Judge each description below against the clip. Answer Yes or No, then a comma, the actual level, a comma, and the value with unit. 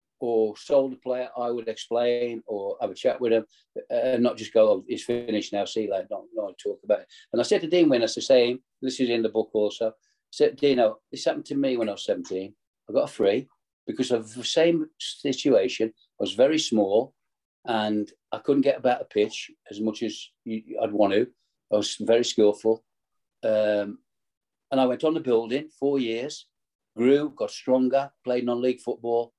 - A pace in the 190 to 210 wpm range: Yes, average, 200 wpm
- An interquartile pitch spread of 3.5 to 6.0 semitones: Yes, average, 3.8 semitones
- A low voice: Yes, low, 120 Hz